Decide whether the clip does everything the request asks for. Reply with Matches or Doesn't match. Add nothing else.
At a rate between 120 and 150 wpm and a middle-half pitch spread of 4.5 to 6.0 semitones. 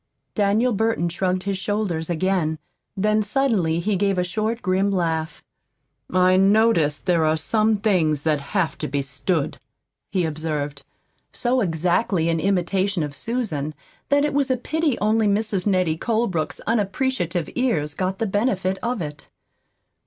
Matches